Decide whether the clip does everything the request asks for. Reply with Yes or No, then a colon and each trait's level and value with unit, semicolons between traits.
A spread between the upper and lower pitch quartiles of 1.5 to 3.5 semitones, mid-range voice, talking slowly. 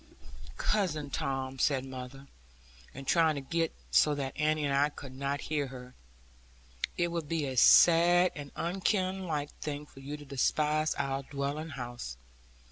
No: average, 2.8 semitones; medium, 145 Hz; average, 150 wpm